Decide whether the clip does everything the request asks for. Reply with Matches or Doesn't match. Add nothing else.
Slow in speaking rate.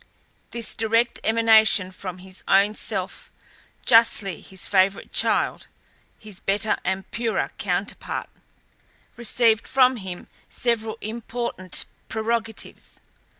Matches